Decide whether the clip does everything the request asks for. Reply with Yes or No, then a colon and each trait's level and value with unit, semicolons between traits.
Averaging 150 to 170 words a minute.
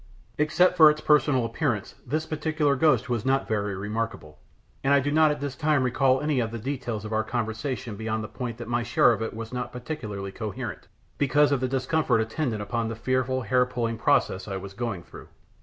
No: fast, 205 wpm